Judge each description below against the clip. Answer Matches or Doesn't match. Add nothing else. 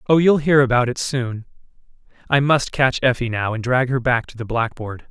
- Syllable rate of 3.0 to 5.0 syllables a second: Doesn't match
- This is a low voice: Matches